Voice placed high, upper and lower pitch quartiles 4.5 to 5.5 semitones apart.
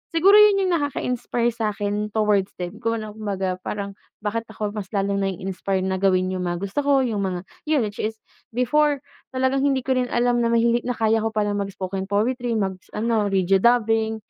No: high, 215 Hz; average, 3.7 semitones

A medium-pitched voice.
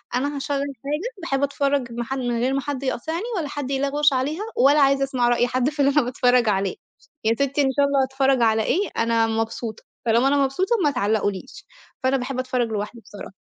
No: very high, 265 Hz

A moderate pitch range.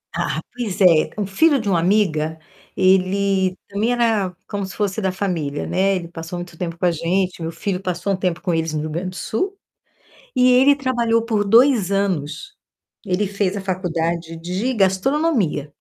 Yes: average, 3.7 semitones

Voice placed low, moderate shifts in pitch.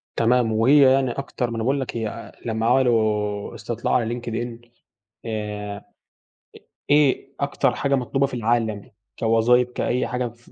No: low, 120 Hz; narrow, 2.3 semitones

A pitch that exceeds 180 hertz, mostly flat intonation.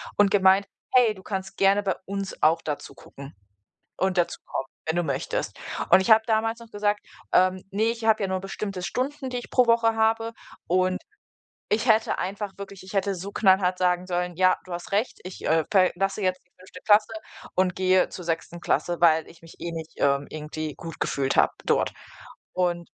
No: high, 190 Hz; average, 3.2 semitones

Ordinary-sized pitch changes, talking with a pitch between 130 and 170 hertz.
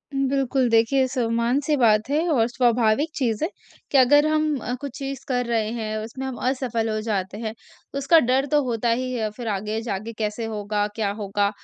No: average, 3.6 semitones; high, 235 Hz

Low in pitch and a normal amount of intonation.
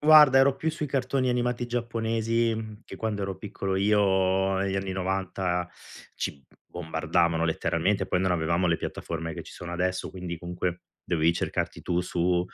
Yes: very low, 95 Hz; average, 4.3 semitones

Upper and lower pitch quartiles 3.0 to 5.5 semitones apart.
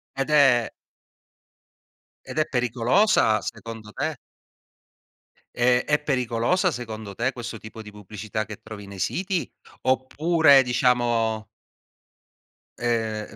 Yes: average, 3.7 semitones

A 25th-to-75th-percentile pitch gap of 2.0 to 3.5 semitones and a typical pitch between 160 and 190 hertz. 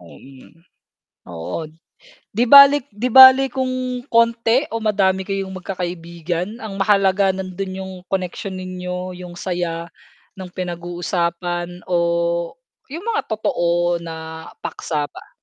No: average, 3.9 semitones; medium, 185 Hz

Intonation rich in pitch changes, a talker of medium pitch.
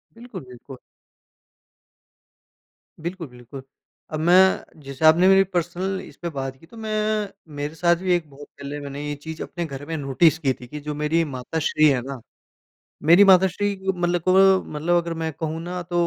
No: average, 4.1 semitones; medium, 165 Hz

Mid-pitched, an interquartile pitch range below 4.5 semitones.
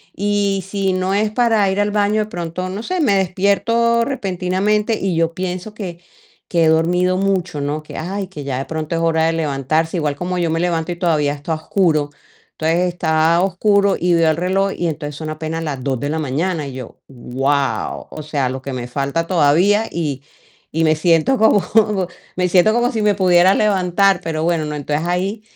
Yes: medium, 175 Hz; average, 4.0 semitones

